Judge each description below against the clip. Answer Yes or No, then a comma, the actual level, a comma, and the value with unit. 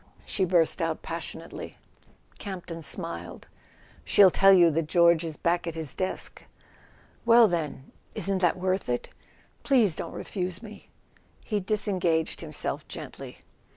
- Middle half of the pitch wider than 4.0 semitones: No, average, 3.0 semitones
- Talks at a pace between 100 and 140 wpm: Yes, slow, 135 wpm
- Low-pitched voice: No, medium, 175 Hz